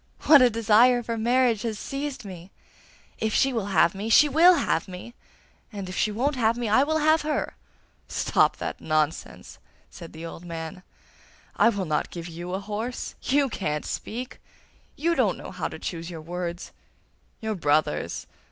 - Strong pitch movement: Yes, wide, 6.4 semitones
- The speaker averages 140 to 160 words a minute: No, average, 175 wpm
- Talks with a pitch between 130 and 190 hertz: No, high, 215 Hz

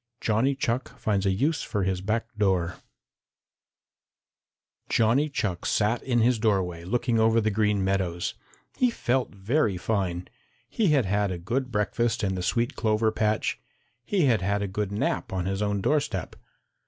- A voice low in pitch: Yes, low, 105 Hz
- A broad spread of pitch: No, average, 3.7 semitones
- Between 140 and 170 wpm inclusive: Yes, average, 165 wpm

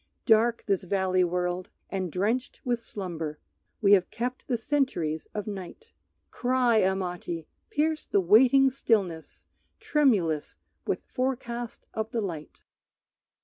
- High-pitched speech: Yes, high, 205 Hz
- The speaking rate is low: Yes, slow, 120 wpm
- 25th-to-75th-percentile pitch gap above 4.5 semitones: Yes, wide, 5.4 semitones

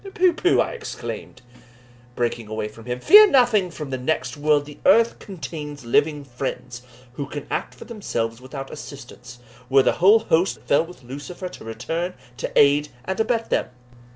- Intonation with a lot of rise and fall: Yes, wide, 6.8 semitones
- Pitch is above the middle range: No, medium, 145 Hz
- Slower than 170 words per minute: No, average, 175 wpm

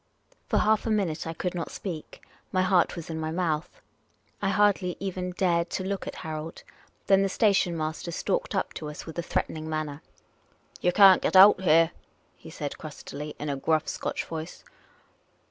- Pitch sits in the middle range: Yes, medium, 170 Hz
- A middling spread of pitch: Yes, average, 3.4 semitones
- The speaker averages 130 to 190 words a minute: Yes, average, 185 wpm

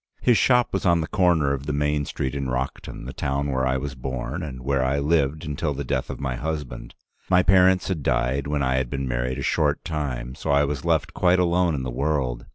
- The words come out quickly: Yes, fast, 235 wpm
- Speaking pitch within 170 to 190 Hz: No, very low, 70 Hz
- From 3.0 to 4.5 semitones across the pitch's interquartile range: Yes, average, 3.4 semitones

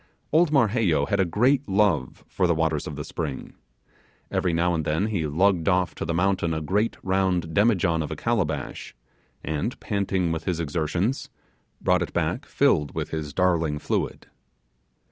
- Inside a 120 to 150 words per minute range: No, average, 165 wpm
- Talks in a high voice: No, very low, 85 Hz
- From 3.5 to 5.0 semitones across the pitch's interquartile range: Yes, average, 4.0 semitones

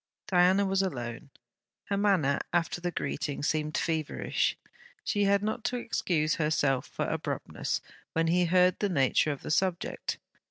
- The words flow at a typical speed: Yes, average, 150 wpm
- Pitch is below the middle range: No, medium, 175 Hz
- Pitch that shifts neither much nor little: Yes, average, 4.1 semitones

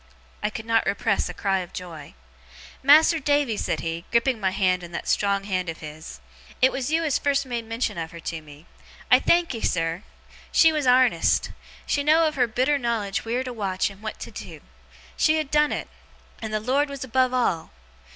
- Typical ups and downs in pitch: No, wide, 6.7 semitones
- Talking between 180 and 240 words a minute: Yes, fast, 205 wpm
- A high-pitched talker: Yes, high, 230 Hz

